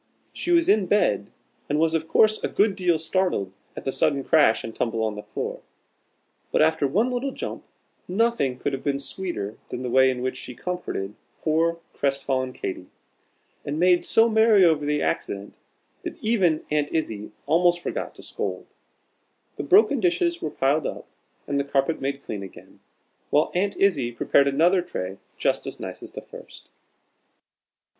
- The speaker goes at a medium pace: Yes, average, 175 wpm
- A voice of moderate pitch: Yes, medium, 155 Hz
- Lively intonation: Yes, wide, 6.1 semitones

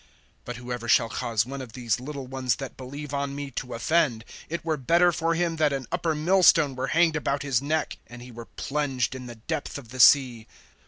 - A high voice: No, low, 135 Hz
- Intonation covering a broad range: No, average, 3.8 semitones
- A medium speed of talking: No, fast, 215 wpm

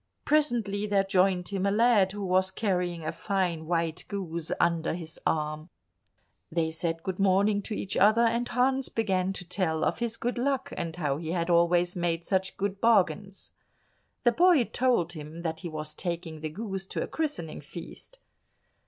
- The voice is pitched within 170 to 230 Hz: Yes, medium, 185 Hz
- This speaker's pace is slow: No, average, 175 wpm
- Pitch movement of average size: Yes, average, 3.8 semitones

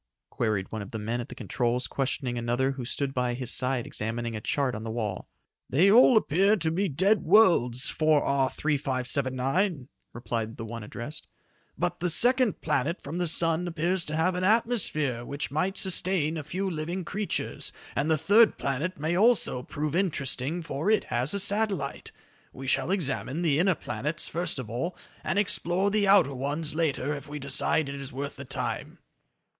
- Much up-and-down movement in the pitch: Yes, wide, 5.9 semitones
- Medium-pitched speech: Yes, medium, 150 Hz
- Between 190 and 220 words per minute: No, average, 180 wpm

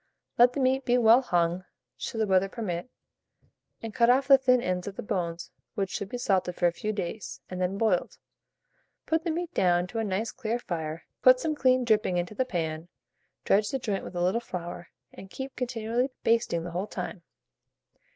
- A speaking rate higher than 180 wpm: Yes, average, 200 wpm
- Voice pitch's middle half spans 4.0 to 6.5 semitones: Yes, wide, 5.6 semitones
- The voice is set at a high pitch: Yes, high, 210 Hz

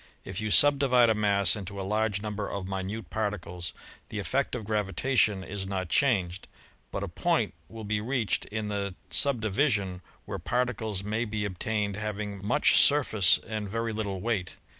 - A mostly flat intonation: Yes, narrow, 2.2 semitones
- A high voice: No, low, 105 Hz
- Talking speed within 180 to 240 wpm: No, average, 165 wpm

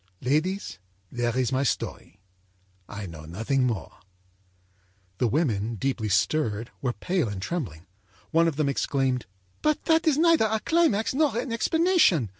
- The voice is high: No, medium, 140 Hz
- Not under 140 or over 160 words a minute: Yes, average, 145 wpm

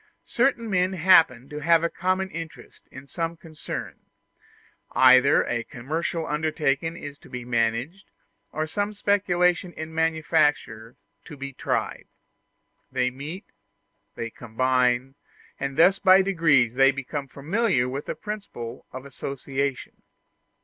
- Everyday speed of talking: No, slow, 125 wpm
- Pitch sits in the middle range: Yes, medium, 150 Hz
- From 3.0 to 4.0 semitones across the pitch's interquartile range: No, average, 5.1 semitones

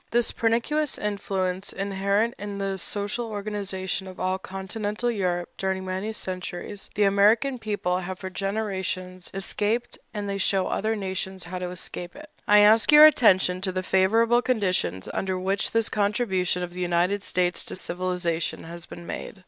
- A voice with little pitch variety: Yes, narrow, 2.3 semitones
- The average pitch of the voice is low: No, high, 195 Hz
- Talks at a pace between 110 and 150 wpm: No, average, 160 wpm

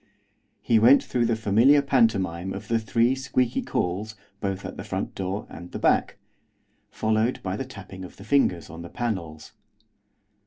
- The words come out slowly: No, average, 165 wpm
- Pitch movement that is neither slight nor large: Yes, average, 4.1 semitones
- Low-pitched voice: Yes, low, 110 Hz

